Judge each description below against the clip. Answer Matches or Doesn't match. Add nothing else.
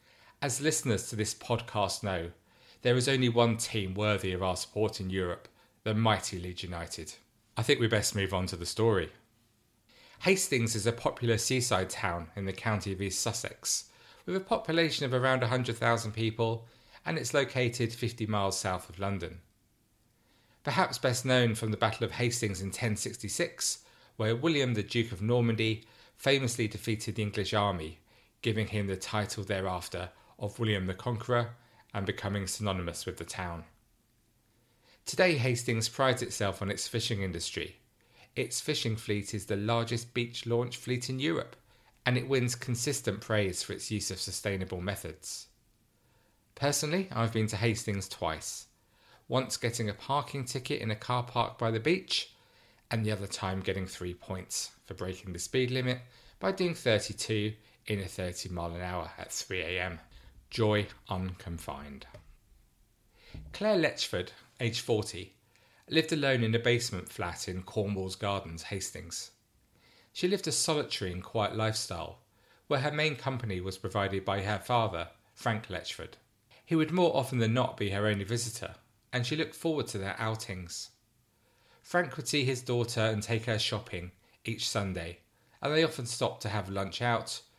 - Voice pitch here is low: Matches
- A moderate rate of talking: Matches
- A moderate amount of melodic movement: Matches